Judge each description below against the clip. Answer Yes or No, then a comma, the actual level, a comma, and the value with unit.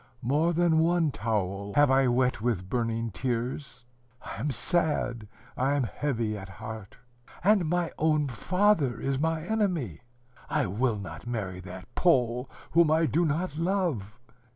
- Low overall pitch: Yes, low, 130 Hz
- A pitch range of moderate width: No, wide, 6.3 semitones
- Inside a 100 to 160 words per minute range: Yes, average, 150 wpm